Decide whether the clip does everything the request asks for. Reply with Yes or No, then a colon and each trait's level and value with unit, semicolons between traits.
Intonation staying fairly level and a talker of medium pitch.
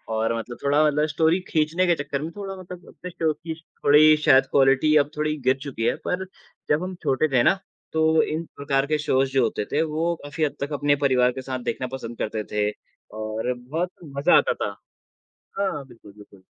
No: average, 3.8 semitones; medium, 145 Hz